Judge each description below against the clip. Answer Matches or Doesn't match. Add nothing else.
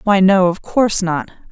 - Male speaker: Doesn't match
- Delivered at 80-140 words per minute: Doesn't match